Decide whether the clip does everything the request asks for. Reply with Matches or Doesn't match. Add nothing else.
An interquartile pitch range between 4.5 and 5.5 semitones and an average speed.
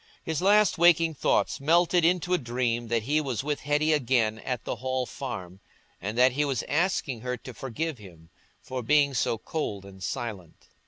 Matches